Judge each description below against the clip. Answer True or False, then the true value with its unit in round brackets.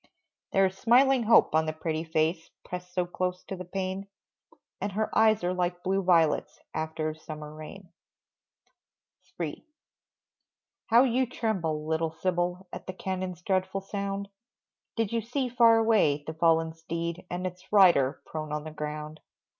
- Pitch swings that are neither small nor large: True (3.6 semitones)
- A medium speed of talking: True (155 wpm)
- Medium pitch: True (180 Hz)